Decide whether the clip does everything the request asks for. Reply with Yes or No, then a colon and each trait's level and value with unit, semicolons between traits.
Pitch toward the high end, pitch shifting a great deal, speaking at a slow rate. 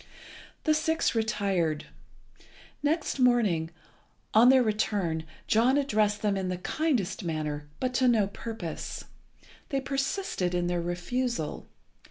Yes: high, 215 Hz; wide, 6.5 semitones; slow, 120 wpm